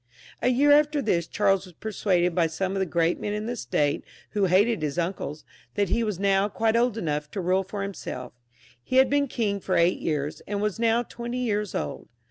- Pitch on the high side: Yes, high, 195 Hz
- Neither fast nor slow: No, fast, 215 wpm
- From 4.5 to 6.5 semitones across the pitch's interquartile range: Yes, average, 4.8 semitones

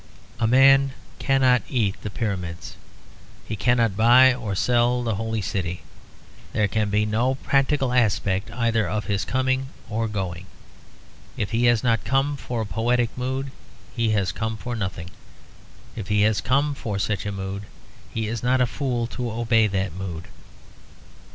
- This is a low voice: Yes, low, 115 Hz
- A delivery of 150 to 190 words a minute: Yes, average, 160 wpm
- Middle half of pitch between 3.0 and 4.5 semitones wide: Yes, average, 3.5 semitones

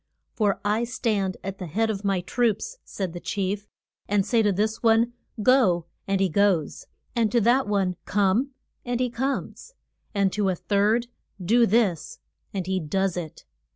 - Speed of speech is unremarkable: Yes, average, 170 wpm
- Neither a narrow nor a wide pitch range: Yes, average, 3.5 semitones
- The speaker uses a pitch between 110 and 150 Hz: No, high, 205 Hz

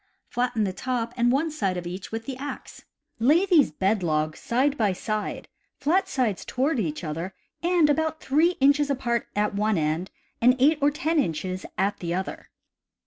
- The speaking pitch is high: Yes, high, 235 Hz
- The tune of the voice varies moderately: No, wide, 7.3 semitones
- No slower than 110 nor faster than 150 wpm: No, average, 180 wpm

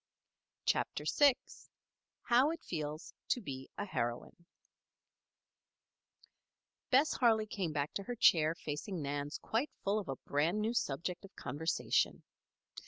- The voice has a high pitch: No, medium, 180 Hz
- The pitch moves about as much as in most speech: No, wide, 7.3 semitones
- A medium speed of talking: No, slow, 125 wpm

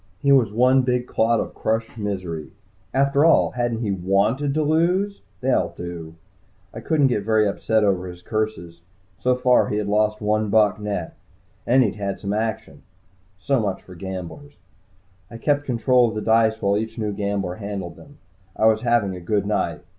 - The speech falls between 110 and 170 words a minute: No, average, 185 wpm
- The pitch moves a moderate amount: Yes, average, 3.9 semitones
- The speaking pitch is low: Yes, low, 110 Hz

